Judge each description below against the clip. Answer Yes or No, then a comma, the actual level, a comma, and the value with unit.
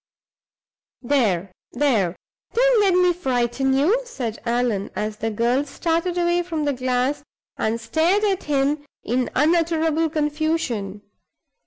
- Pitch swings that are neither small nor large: No, wide, 5.9 semitones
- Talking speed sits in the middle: No, slow, 125 wpm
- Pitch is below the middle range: No, very high, 285 Hz